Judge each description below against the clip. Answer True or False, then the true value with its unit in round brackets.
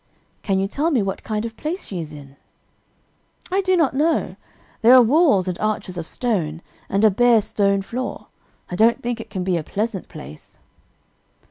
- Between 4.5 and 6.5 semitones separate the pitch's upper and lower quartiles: True (4.9 semitones)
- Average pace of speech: True (190 wpm)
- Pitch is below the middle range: False (215 Hz)